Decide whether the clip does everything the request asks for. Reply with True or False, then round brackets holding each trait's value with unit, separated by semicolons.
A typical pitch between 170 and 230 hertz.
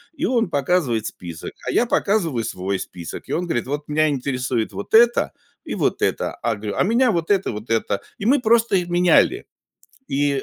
False (150 Hz)